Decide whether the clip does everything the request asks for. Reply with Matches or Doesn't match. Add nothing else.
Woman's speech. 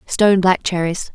Matches